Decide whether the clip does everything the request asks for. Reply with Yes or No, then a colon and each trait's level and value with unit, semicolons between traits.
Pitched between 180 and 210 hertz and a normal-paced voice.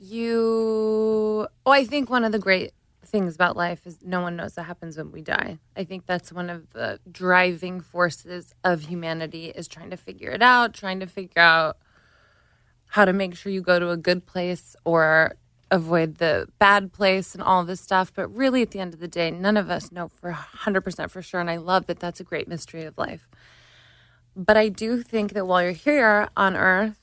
No: medium, 185 Hz; fast, 215 wpm